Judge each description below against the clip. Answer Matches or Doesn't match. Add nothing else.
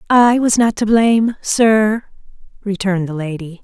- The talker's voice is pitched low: Doesn't match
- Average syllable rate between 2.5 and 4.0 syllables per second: Doesn't match